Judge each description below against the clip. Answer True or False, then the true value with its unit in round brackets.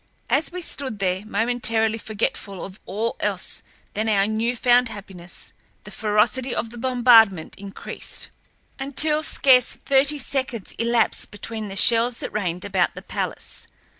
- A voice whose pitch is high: True (225 Hz)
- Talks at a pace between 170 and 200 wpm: False (140 wpm)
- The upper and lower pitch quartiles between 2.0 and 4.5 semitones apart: True (3.6 semitones)